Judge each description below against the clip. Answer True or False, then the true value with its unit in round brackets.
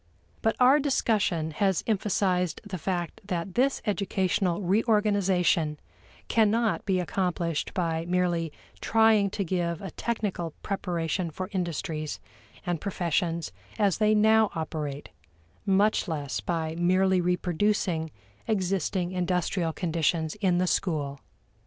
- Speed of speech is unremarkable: False (115 wpm)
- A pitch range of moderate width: True (3.4 semitones)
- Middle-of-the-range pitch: True (180 Hz)